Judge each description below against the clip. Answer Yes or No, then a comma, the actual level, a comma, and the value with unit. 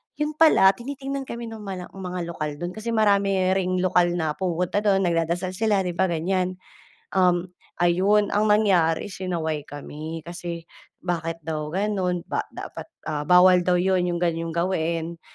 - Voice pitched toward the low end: No, medium, 180 Hz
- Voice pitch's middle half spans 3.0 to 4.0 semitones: No, narrow, 2.5 semitones